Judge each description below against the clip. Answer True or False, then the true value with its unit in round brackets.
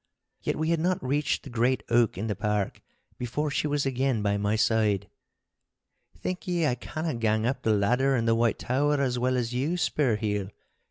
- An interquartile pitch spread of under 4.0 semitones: False (4.7 semitones)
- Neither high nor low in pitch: False (125 Hz)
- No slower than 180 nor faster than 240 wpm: True (195 wpm)